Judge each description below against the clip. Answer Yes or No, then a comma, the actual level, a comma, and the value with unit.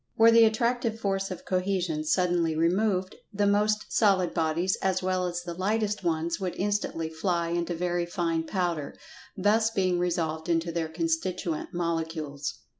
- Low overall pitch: No, medium, 175 Hz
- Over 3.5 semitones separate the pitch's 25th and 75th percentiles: No, average, 3.1 semitones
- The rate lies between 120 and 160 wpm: Yes, average, 150 wpm